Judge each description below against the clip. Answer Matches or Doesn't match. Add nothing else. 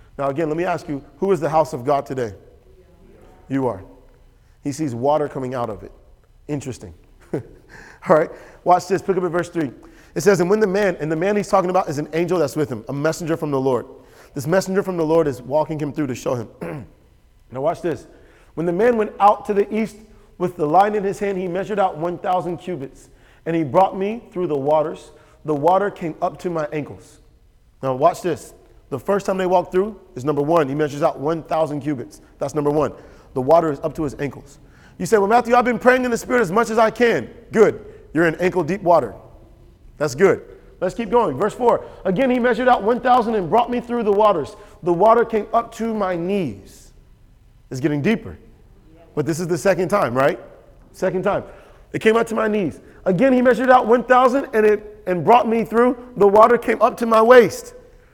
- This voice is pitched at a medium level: Matches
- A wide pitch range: Matches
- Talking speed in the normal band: Doesn't match